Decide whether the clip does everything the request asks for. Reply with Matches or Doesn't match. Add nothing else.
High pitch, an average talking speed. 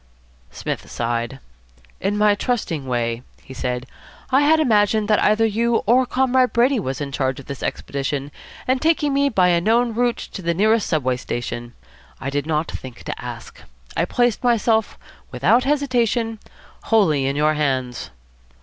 Matches